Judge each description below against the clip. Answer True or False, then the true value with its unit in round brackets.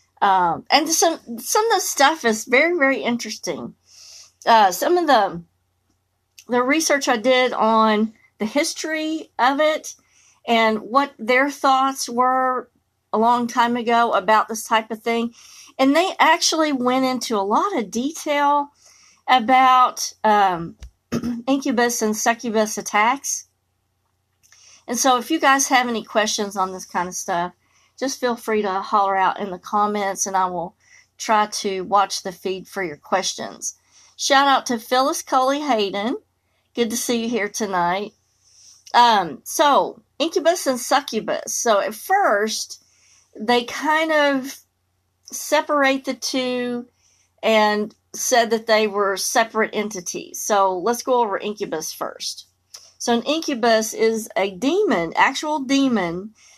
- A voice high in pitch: True (235 Hz)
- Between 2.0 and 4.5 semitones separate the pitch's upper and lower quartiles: False (4.9 semitones)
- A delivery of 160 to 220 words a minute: False (140 wpm)